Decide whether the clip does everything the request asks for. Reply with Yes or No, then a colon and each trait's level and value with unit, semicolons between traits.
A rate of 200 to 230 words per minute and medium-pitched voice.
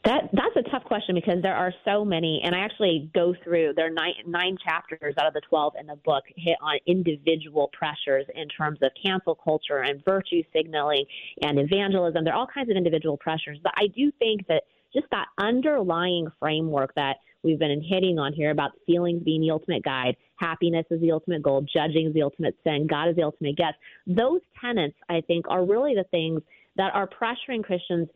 Yes: fast, 205 wpm; medium, 165 Hz